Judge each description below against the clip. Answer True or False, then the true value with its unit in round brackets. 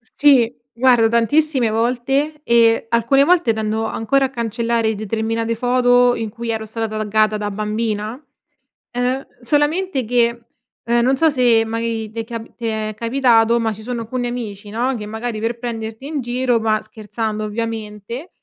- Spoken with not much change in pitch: True (2.0 semitones)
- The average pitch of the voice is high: True (230 Hz)